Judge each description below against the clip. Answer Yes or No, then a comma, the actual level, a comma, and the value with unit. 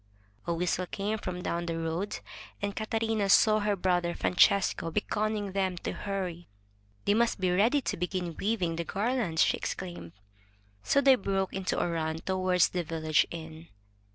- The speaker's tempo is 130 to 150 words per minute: No, average, 160 wpm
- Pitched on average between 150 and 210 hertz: Yes, medium, 185 Hz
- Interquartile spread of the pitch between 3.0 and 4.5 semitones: Yes, average, 3.4 semitones